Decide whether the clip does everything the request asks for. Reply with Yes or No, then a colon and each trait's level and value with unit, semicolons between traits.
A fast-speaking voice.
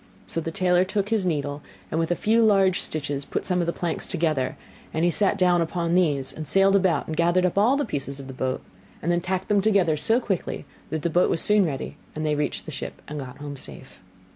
Yes: fast, 245 wpm